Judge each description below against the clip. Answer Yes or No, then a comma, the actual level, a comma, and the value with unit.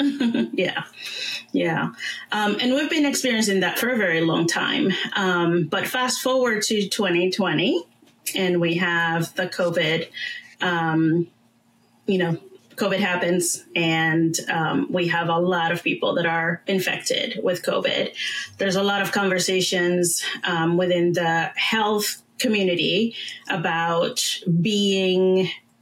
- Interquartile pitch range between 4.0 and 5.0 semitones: No, average, 3.5 semitones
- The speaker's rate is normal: No, slow, 125 wpm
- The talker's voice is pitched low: No, medium, 180 Hz